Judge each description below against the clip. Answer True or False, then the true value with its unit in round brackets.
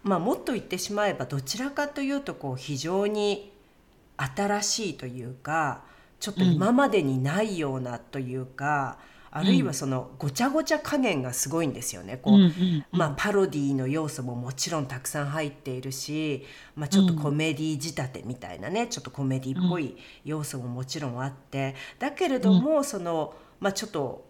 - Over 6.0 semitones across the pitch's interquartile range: True (7.1 semitones)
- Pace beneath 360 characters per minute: False (375 characters per minute)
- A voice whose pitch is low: False (155 Hz)